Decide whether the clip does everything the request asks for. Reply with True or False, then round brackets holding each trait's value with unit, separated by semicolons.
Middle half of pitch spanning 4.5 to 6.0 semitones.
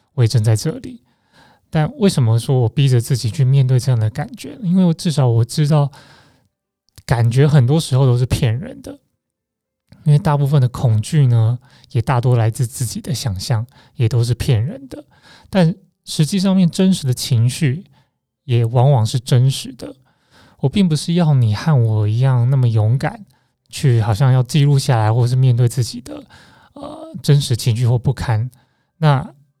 False (3.8 semitones)